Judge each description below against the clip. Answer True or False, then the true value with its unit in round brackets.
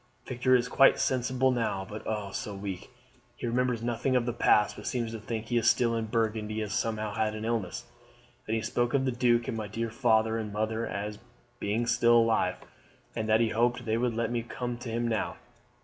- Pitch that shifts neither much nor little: False (1.8 semitones)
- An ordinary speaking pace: False (220 wpm)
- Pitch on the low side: True (115 Hz)